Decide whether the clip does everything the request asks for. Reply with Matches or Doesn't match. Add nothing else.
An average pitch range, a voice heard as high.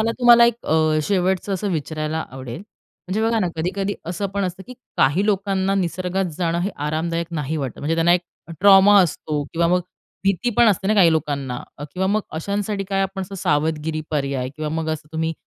Doesn't match